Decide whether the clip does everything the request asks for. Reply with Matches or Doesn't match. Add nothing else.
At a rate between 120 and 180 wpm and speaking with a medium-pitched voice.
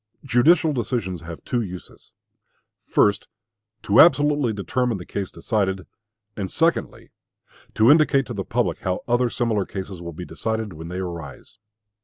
Doesn't match